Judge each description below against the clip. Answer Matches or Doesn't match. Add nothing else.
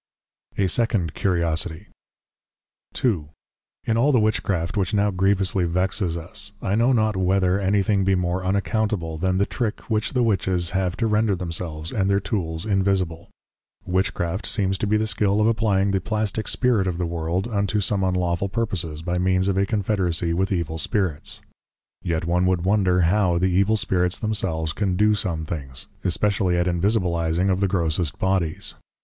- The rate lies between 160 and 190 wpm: Matches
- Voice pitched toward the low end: Matches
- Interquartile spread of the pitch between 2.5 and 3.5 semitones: Matches